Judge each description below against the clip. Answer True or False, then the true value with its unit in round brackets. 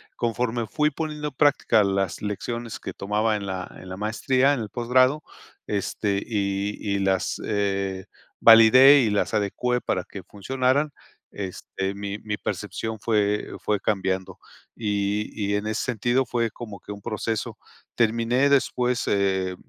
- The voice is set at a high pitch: False (105 Hz)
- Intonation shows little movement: False (3.6 semitones)